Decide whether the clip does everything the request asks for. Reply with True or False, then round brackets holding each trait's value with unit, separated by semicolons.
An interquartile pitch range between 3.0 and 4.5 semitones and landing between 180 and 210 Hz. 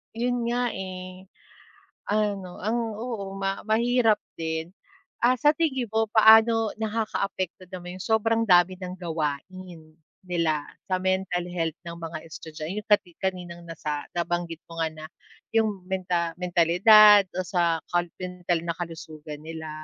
True (4.1 semitones; 185 Hz)